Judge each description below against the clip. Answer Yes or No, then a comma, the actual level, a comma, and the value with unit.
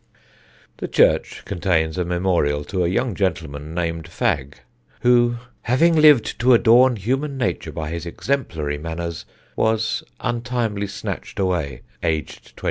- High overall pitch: No, very low, 95 Hz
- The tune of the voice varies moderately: No, wide, 6.8 semitones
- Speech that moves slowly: Yes, slow, 130 wpm